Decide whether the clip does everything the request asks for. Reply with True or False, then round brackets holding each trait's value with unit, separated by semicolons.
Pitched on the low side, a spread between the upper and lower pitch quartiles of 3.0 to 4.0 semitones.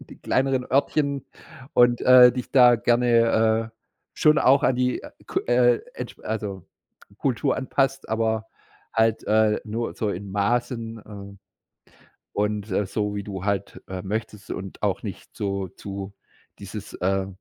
True (110 Hz; 3.4 semitones)